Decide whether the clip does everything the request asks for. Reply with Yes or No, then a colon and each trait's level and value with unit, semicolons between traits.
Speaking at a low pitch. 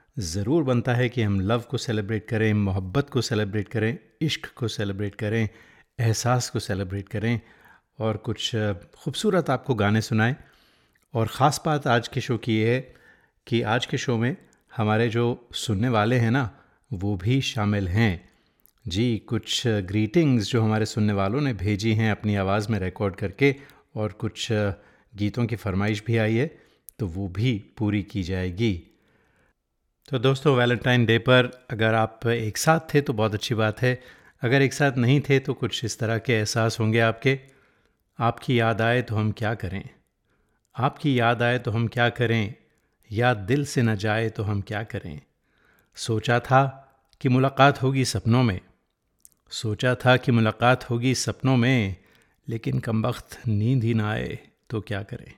Yes: low, 115 Hz